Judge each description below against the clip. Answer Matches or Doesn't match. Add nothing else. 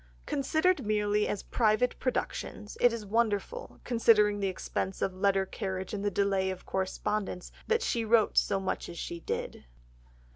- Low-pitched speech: Doesn't match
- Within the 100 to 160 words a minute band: Matches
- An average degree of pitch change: Matches